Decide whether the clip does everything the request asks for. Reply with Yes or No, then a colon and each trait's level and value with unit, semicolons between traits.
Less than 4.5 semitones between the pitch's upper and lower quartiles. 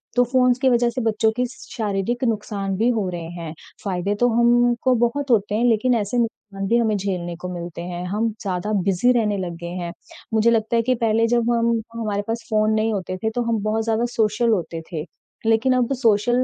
Yes: average, 3.3 semitones